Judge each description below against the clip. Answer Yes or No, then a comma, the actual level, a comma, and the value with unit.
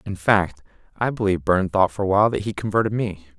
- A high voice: No, low, 100 Hz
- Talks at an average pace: No, fast, 230 wpm